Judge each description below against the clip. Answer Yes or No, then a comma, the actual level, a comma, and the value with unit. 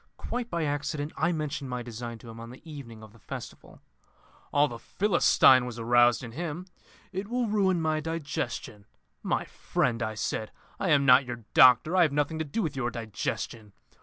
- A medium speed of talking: Yes, average, 190 wpm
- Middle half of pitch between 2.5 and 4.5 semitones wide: No, average, 5.3 semitones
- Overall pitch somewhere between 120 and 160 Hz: Yes, medium, 140 Hz